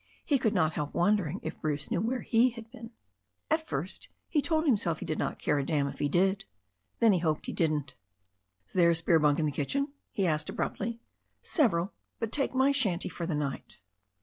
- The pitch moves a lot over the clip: Yes, wide, 7.3 semitones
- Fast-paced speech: Yes, fast, 215 wpm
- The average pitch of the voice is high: No, medium, 180 Hz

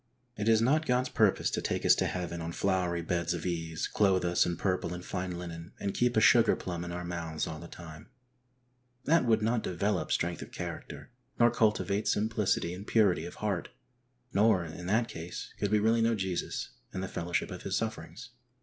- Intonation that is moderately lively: Yes, average, 4.1 semitones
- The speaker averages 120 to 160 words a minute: No, average, 200 wpm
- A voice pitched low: Yes, very low, 95 Hz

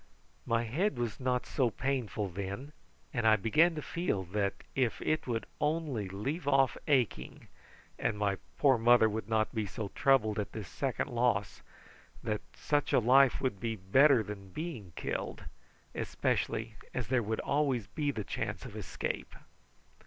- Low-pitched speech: Yes, low, 120 Hz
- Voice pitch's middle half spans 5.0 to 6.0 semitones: No, average, 4.5 semitones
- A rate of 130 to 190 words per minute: Yes, average, 155 wpm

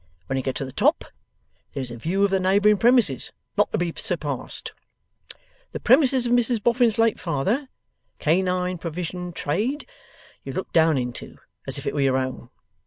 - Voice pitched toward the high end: No, medium, 180 Hz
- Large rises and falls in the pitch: Yes, wide, 8.4 semitones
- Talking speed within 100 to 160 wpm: No, average, 175 wpm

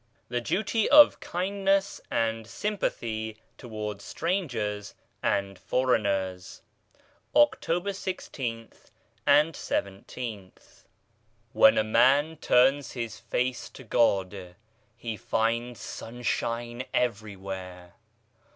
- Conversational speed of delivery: No, slow, 85 wpm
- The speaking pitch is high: No, low, 115 Hz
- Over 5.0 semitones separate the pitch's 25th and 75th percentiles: Yes, wide, 5.6 semitones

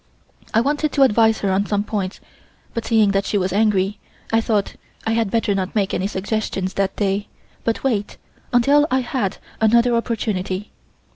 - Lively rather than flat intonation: No, average, 2.9 semitones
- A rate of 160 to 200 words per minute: Yes, average, 170 wpm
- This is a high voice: Yes, high, 215 Hz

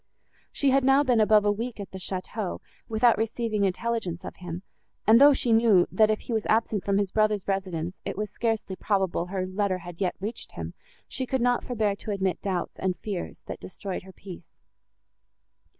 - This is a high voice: Yes, high, 205 Hz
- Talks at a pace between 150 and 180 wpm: No, average, 195 wpm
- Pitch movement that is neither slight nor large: Yes, average, 3.2 semitones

